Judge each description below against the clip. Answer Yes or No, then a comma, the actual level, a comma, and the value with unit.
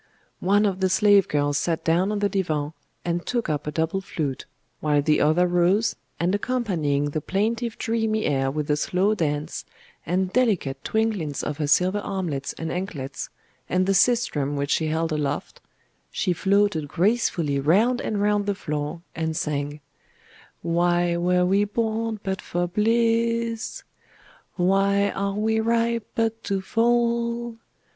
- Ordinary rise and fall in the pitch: No, wide, 5.7 semitones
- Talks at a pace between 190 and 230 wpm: No, average, 150 wpm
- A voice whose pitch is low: No, medium, 185 Hz